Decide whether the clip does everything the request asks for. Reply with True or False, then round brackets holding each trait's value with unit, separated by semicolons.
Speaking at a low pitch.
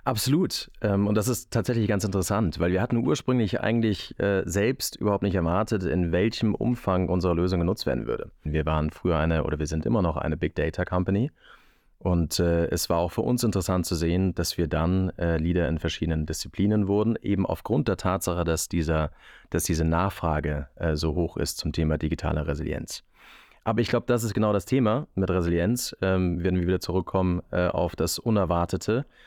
True (90 Hz)